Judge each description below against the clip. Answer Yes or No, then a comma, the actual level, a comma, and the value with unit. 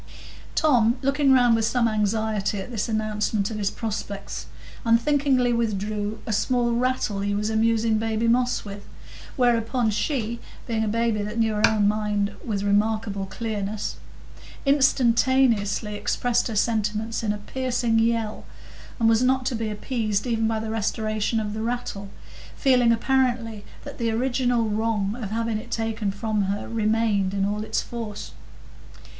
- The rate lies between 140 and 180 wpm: Yes, average, 150 wpm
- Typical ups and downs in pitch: No, narrow, 2.1 semitones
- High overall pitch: Yes, high, 225 Hz